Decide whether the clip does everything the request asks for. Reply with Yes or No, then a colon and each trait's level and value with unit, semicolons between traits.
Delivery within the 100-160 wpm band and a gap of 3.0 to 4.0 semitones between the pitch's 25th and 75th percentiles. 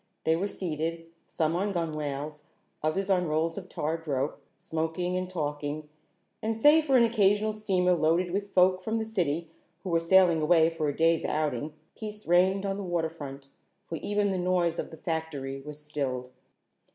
No: average, 175 wpm; average, 3.6 semitones